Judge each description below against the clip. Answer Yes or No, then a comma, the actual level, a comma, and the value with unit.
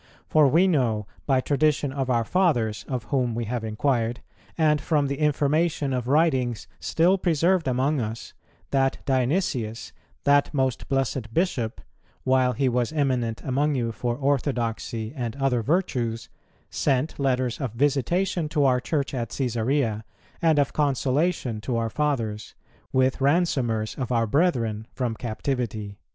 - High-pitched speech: No, low, 130 Hz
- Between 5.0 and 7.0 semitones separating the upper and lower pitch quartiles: No, average, 3.8 semitones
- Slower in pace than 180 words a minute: Yes, average, 140 wpm